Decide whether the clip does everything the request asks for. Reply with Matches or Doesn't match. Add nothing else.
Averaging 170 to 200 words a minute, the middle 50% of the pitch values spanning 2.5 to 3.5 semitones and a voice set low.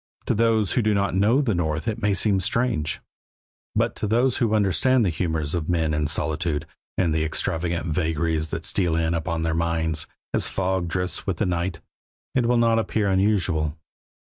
Doesn't match